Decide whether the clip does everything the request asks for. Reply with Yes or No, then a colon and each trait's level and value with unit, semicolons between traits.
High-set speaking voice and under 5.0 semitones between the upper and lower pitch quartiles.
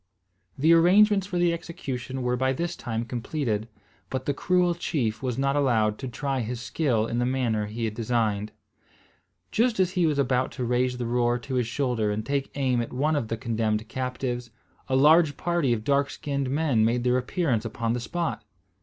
No: low, 125 Hz; average, 3.8 semitones